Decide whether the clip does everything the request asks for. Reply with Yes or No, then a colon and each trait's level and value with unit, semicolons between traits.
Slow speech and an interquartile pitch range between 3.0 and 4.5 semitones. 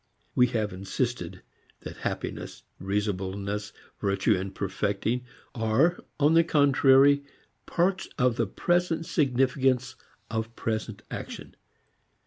No: slow, 100 wpm; wide, 5.4 semitones